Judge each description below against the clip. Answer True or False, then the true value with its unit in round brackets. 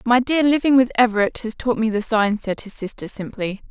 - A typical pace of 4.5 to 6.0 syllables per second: True (5.5 syllables/s)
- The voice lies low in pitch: False (230 Hz)